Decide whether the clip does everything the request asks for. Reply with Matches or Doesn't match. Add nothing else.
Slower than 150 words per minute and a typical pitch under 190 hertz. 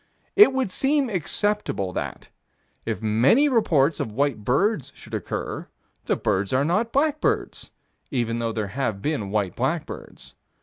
Matches